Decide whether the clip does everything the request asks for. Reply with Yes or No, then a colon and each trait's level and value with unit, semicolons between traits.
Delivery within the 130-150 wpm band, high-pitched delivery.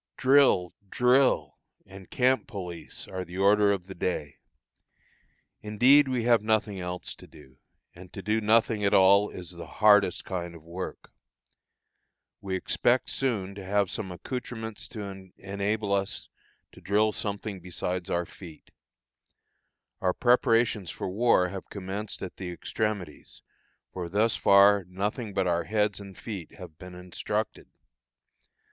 No: average, 140 wpm; low, 100 Hz